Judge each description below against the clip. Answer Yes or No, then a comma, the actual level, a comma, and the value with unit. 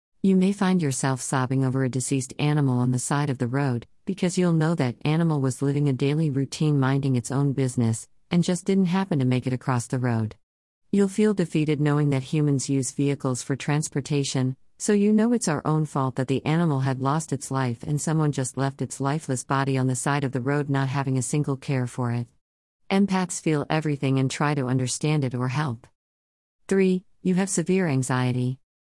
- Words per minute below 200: No, fast, 205 wpm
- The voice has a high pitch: No, medium, 140 Hz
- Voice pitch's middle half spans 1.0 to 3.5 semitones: Yes, average, 3.2 semitones